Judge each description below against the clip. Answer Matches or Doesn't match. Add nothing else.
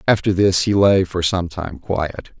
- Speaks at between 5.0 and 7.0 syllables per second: Doesn't match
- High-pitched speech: Doesn't match